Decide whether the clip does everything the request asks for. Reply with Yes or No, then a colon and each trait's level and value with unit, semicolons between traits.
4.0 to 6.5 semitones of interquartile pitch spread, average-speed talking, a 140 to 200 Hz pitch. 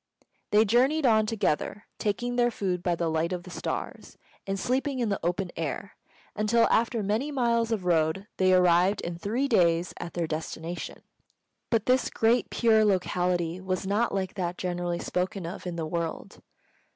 Yes: average, 4.6 semitones; average, 170 wpm; high, 190 Hz